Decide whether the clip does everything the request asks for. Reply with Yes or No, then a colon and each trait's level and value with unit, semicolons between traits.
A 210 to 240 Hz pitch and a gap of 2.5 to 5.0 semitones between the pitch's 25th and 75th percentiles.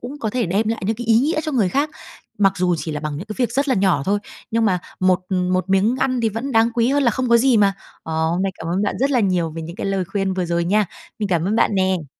No: high, 200 Hz; average, 4.4 semitones